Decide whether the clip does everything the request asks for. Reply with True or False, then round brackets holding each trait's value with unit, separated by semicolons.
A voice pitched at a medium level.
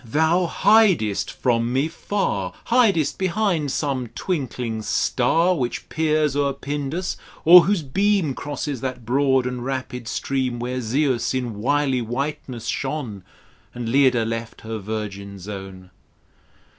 False (130 Hz)